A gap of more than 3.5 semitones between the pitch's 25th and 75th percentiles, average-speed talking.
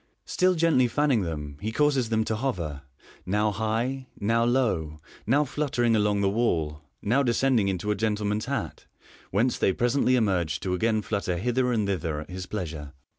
Yes: average, 5.0 semitones; average, 170 wpm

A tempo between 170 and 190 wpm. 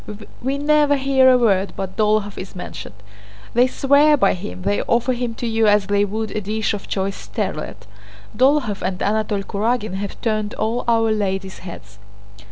Yes: average, 175 wpm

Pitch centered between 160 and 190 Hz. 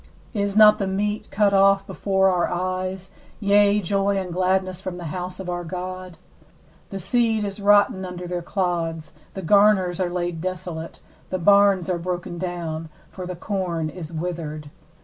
Yes: medium, 185 Hz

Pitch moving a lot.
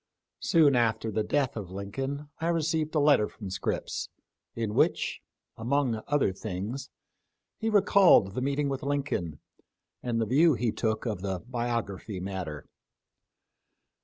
Yes: wide, 6.0 semitones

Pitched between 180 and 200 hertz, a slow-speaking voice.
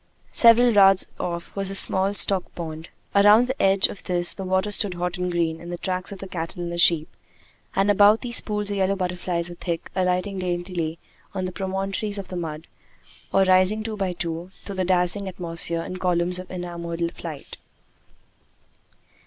No: medium, 185 Hz; average, 185 wpm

